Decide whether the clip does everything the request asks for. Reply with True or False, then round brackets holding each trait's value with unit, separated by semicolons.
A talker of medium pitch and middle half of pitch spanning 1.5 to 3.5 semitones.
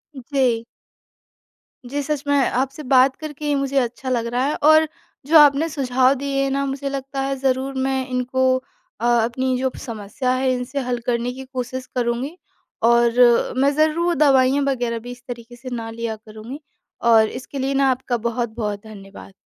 False (260 Hz; 2.4 semitones)